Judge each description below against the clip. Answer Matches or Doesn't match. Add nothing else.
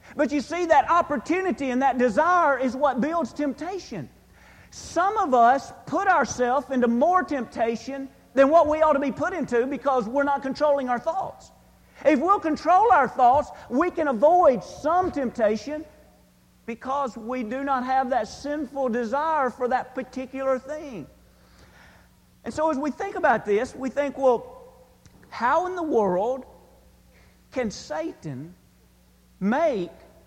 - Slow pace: Doesn't match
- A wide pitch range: Doesn't match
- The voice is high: Matches